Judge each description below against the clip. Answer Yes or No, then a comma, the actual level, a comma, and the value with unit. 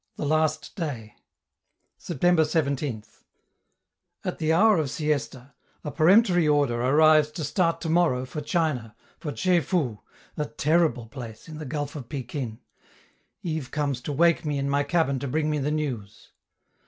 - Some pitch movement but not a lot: Yes, average, 3.5 semitones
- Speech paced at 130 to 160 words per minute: Yes, average, 155 wpm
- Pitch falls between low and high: Yes, medium, 150 Hz